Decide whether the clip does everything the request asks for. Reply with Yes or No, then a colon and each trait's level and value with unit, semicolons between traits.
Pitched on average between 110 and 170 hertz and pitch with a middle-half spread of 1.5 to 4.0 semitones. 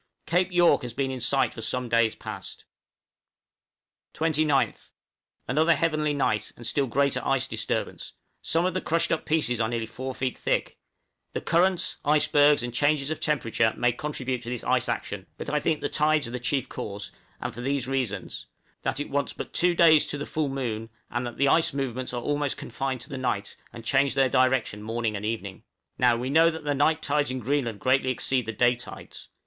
Yes: low, 135 Hz; average, 3.7 semitones